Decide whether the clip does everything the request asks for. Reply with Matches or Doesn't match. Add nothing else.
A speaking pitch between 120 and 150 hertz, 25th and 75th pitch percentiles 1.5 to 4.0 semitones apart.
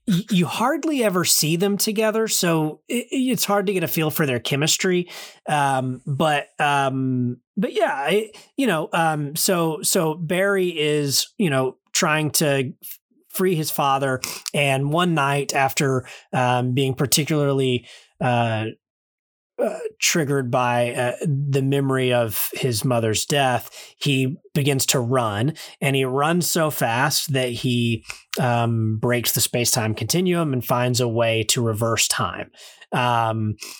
Doesn't match